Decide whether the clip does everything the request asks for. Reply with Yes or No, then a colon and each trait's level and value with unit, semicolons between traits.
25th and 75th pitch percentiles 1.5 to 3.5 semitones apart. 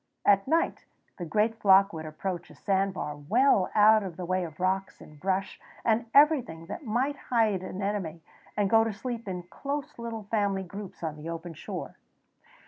No: average, 4.1 semitones